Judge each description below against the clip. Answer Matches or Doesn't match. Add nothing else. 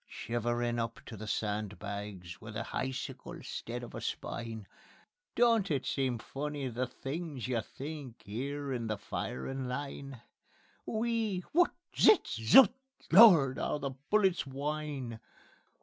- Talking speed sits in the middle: Doesn't match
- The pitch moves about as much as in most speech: Matches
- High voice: Doesn't match